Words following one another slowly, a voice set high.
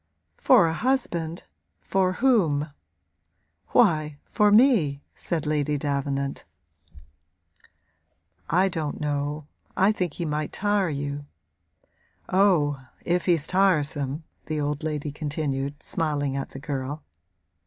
No: slow, 110 wpm; medium, 150 Hz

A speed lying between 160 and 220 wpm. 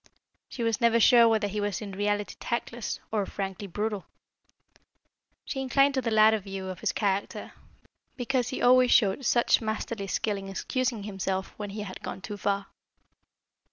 Yes: average, 165 wpm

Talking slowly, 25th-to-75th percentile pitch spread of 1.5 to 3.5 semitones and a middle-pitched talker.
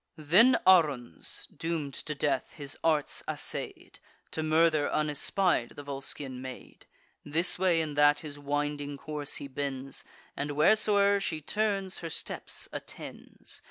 Yes: slow, 130 wpm; average, 2.8 semitones; medium, 150 Hz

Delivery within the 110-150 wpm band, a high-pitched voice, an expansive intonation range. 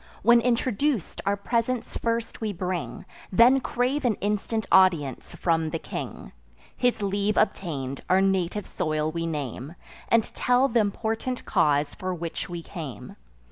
Yes: average, 140 wpm; high, 195 Hz; wide, 5.9 semitones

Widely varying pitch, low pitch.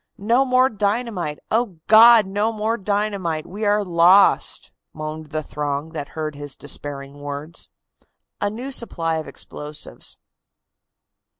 No: wide, 6.0 semitones; medium, 185 Hz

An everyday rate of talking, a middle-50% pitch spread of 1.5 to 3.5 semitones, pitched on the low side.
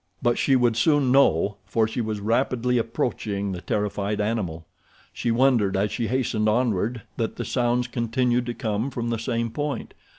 Yes: average, 170 wpm; average, 2.8 semitones; low, 115 Hz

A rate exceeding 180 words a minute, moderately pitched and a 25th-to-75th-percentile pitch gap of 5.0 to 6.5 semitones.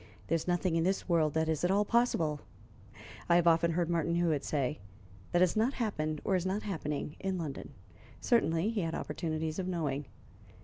No: average, 190 wpm; medium, 170 Hz; average, 3.0 semitones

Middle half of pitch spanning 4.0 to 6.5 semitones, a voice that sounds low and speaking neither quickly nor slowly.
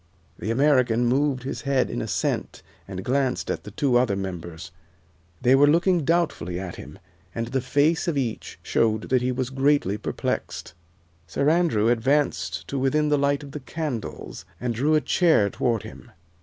Yes: average, 4.5 semitones; low, 130 Hz; average, 170 wpm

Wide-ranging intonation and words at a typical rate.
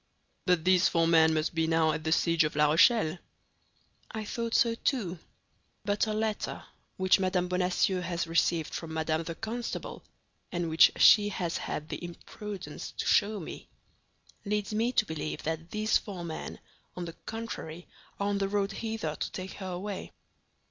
No: average, 4.2 semitones; average, 170 wpm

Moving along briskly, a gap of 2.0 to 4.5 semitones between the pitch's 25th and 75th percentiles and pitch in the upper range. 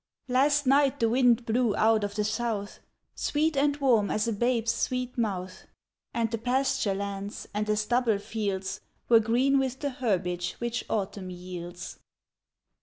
No: average, 155 wpm; average, 3.9 semitones; high, 225 Hz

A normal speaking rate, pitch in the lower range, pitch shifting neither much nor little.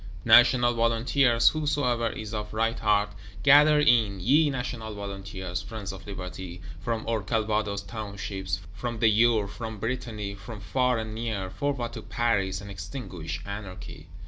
Yes: average, 145 wpm; low, 110 Hz; average, 3.1 semitones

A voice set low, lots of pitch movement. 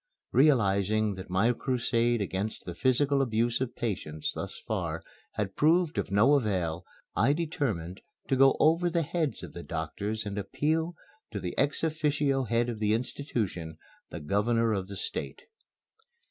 Yes: low, 115 Hz; wide, 6.1 semitones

